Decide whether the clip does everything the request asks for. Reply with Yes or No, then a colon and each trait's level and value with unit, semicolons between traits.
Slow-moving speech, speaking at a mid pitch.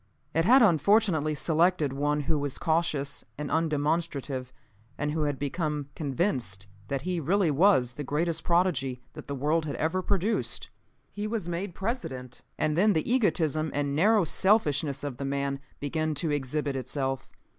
No: average, 155 wpm; medium, 155 Hz